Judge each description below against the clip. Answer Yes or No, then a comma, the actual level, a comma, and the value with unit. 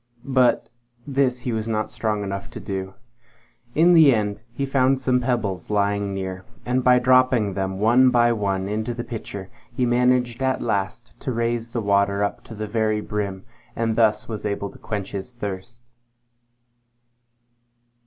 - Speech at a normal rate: Yes, average, 165 wpm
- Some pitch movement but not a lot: Yes, average, 3.6 semitones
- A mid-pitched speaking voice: No, low, 115 Hz